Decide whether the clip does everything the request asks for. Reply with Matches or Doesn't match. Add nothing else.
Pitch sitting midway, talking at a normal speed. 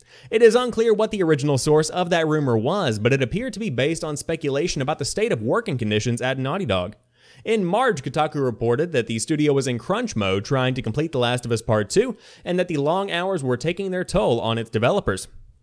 Doesn't match